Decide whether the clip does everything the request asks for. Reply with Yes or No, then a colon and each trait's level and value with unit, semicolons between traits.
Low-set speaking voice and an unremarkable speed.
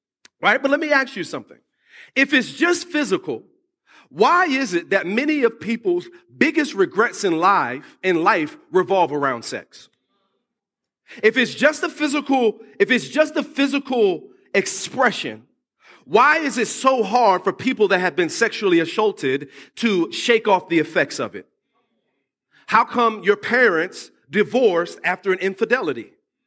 No: high, 245 Hz; average, 145 wpm